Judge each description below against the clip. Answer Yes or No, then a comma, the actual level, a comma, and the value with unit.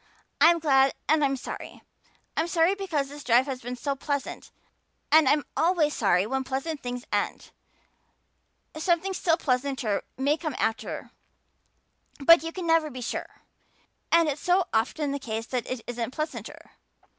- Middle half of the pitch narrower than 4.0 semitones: No, average, 4.3 semitones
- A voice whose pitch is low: No, very high, 285 Hz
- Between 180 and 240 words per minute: No, average, 155 wpm